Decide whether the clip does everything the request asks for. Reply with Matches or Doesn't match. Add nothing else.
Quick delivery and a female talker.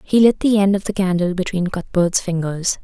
Matches